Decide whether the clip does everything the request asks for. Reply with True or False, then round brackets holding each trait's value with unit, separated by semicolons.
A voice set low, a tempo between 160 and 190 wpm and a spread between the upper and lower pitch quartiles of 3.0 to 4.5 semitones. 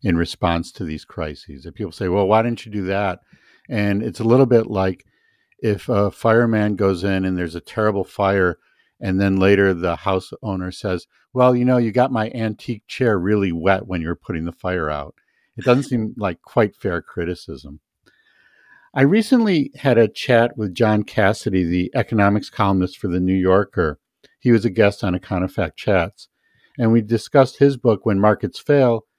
True (105 Hz; 185 wpm; 3.8 semitones)